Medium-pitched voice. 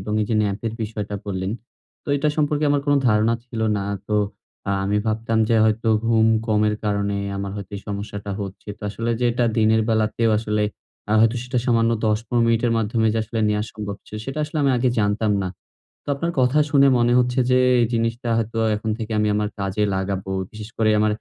No: low, 110 Hz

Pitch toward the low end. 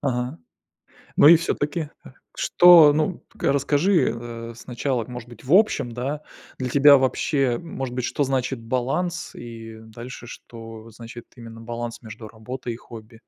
Yes: low, 125 Hz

